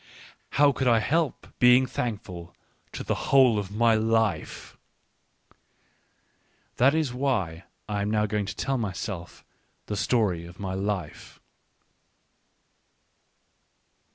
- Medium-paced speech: No, slow, 115 wpm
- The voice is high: No, low, 110 Hz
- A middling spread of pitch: Yes, average, 4.4 semitones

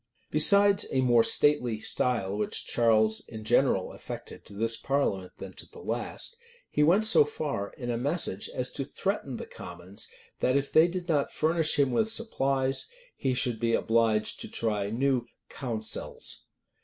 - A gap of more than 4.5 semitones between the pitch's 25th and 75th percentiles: Yes, average, 5.2 semitones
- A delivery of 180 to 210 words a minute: No, average, 165 wpm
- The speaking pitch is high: No, low, 125 Hz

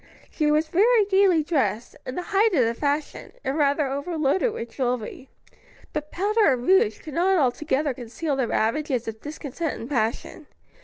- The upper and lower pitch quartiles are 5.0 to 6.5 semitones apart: Yes, wide, 5.4 semitones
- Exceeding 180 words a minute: No, average, 165 wpm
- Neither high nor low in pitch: No, very high, 295 Hz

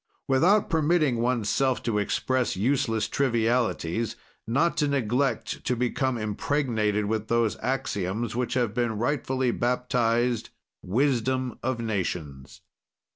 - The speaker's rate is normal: No, slow, 110 wpm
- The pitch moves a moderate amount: Yes, average, 3.1 semitones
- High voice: No, low, 120 Hz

